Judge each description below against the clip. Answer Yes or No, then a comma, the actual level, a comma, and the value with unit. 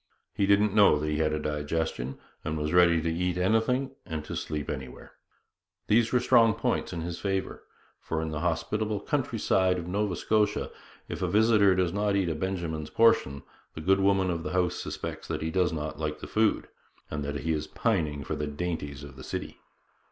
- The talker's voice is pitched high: No, very low, 90 Hz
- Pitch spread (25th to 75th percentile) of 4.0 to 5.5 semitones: Yes, average, 4.9 semitones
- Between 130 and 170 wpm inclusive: No, average, 200 wpm